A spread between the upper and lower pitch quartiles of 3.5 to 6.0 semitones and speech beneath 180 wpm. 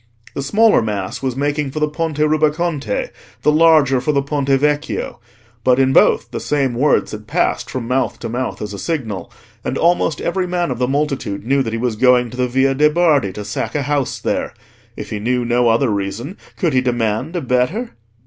No: average, 4.1 semitones; fast, 205 wpm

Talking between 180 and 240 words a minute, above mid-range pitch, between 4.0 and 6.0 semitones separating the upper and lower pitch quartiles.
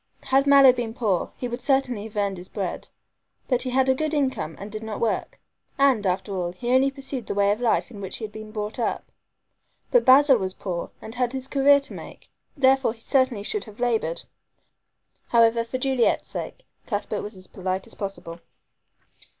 Yes: average, 200 wpm; high, 230 Hz; average, 4.5 semitones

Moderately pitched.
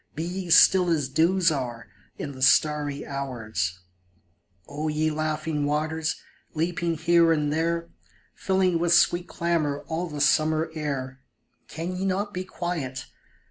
Yes: medium, 155 Hz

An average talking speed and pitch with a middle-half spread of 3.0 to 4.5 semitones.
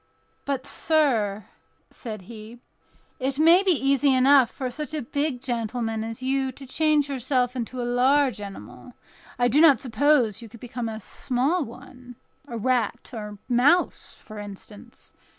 Yes: average, 150 wpm; average, 3.7 semitones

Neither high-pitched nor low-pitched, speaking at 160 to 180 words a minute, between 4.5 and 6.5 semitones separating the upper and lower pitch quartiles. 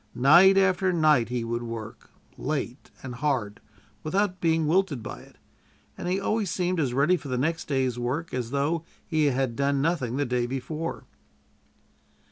Yes: medium, 145 Hz; average, 165 wpm; average, 5.2 semitones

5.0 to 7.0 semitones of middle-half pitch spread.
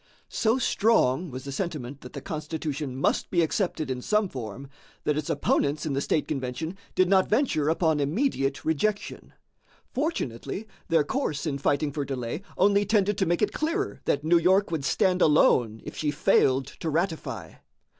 Yes: wide, 5.5 semitones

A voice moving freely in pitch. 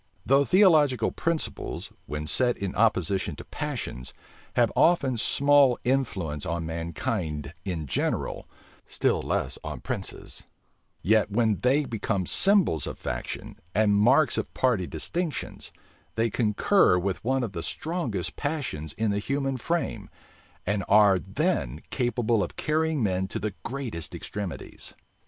Yes: wide, 7.1 semitones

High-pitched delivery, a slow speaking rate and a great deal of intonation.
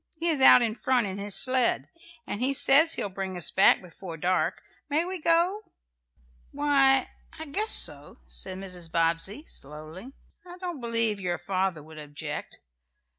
No: high, 215 Hz; average, 160 wpm; wide, 8.1 semitones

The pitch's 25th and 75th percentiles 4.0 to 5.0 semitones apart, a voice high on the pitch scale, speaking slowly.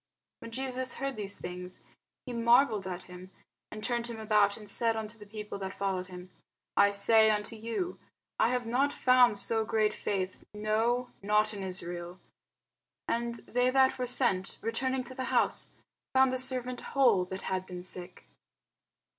No: average, 4.3 semitones; high, 220 Hz; average, 165 wpm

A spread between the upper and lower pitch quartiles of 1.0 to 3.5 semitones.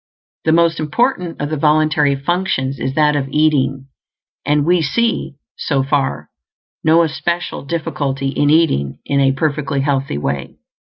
Yes: average, 2.8 semitones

